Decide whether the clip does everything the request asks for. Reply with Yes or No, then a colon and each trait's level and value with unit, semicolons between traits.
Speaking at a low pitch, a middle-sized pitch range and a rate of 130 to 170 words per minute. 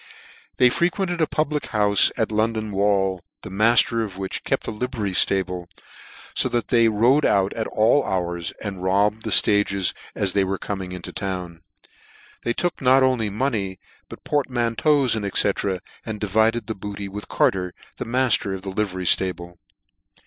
Yes: low, 105 Hz; average, 3.6 semitones; average, 160 wpm